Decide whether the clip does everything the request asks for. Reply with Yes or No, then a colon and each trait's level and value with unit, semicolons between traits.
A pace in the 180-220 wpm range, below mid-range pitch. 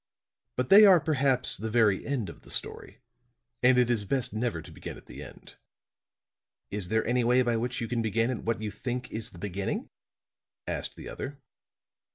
Yes: average, 195 wpm; low, 120 Hz